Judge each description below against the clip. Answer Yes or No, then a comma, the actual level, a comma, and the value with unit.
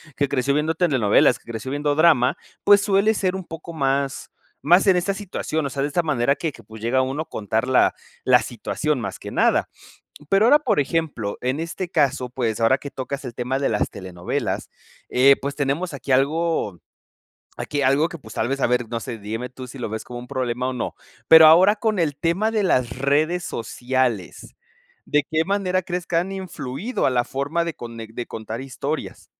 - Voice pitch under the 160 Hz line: Yes, medium, 140 Hz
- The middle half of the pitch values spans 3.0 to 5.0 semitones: No, wide, 5.4 semitones